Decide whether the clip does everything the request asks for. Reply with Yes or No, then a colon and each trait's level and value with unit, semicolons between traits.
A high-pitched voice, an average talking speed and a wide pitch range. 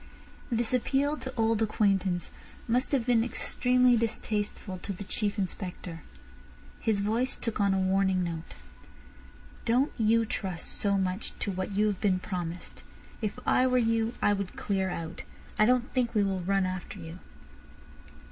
No: high, 205 Hz; average, 155 wpm; average, 3.6 semitones